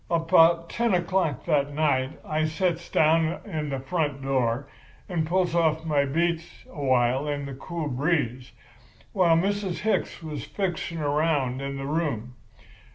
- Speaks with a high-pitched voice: No, medium, 155 Hz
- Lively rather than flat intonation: No, average, 3.5 semitones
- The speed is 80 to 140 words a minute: No, average, 150 wpm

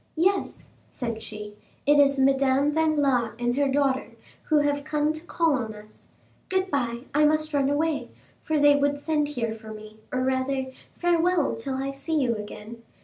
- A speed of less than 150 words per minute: No, average, 170 wpm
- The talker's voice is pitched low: No, very high, 275 Hz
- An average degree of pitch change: Yes, average, 3.7 semitones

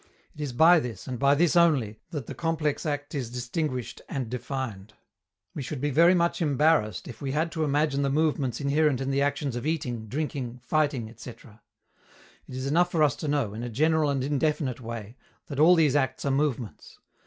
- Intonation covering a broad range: No, average, 3.8 semitones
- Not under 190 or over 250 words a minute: Yes, average, 200 wpm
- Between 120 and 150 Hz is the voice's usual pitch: Yes, medium, 140 Hz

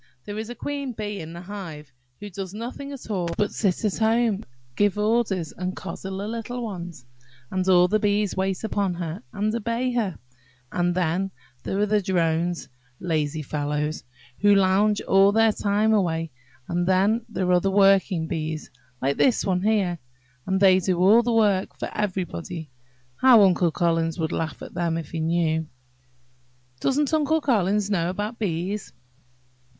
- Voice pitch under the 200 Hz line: Yes, high, 190 Hz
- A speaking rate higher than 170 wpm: No, average, 165 wpm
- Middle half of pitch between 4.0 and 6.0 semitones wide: No, average, 3.6 semitones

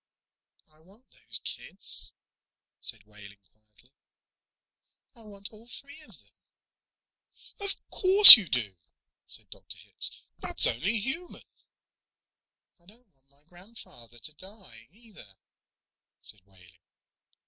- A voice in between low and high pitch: Yes, medium, 175 Hz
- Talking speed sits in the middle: No, slow, 115 wpm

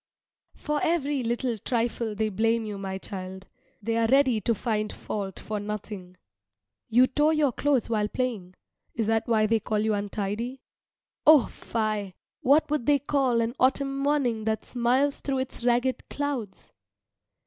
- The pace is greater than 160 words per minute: No, average, 155 wpm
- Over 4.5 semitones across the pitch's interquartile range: No, average, 3.9 semitones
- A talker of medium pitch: No, high, 230 Hz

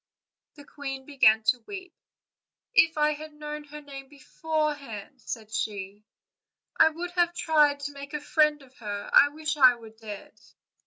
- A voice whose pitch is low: No, very high, 285 Hz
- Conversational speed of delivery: Yes, average, 160 wpm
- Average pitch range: Yes, average, 4.2 semitones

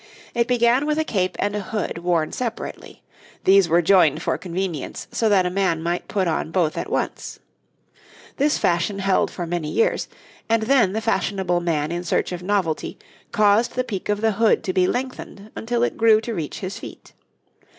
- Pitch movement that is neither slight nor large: Yes, average, 4.4 semitones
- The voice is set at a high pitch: Yes, high, 195 Hz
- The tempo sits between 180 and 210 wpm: Yes, average, 190 wpm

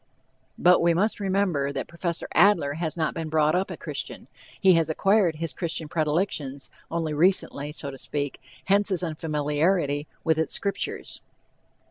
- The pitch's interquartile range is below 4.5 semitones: Yes, average, 3.6 semitones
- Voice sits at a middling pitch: Yes, medium, 165 Hz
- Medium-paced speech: Yes, average, 155 wpm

